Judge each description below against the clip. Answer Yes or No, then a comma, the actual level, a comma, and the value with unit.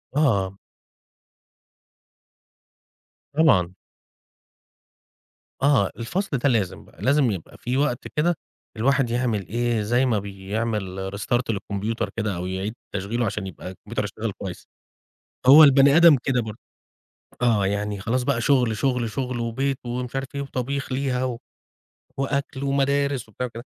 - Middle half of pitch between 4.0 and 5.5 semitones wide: Yes, average, 4.6 semitones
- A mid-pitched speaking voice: No, low, 120 Hz